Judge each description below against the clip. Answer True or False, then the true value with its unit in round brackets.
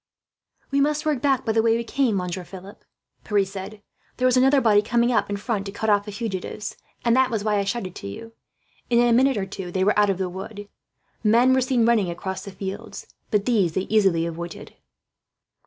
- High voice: True (210 Hz)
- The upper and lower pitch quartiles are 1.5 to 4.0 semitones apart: True (3.6 semitones)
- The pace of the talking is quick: True (215 wpm)